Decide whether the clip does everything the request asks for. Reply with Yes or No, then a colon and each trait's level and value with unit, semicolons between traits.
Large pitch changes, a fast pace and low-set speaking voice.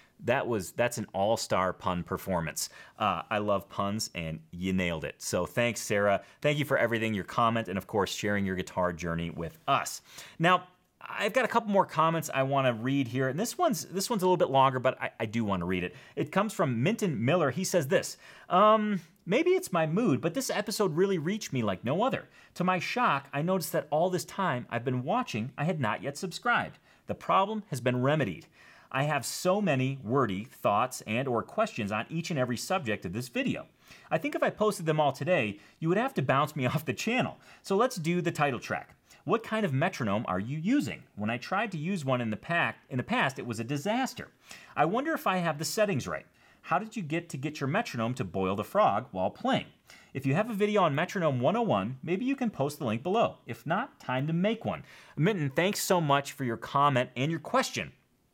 No: wide, 8.1 semitones; fast, 230 wpm; medium, 150 Hz